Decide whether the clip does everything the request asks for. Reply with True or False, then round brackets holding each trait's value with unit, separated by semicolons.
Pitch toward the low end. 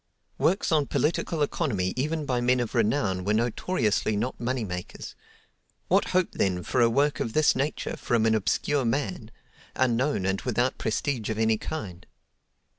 True (120 Hz)